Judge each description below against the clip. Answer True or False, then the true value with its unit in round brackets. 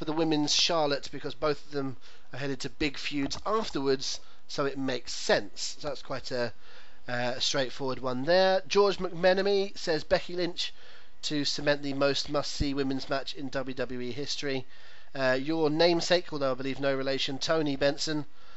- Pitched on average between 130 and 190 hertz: True (140 Hz)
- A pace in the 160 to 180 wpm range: True (170 wpm)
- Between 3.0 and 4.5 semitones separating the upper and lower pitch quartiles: True (3.4 semitones)